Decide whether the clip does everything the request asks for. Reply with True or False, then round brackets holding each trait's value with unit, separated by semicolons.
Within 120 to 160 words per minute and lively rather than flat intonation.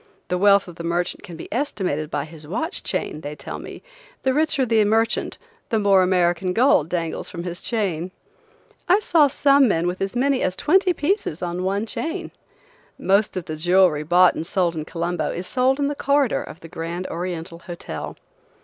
False (190 wpm; 6.4 semitones)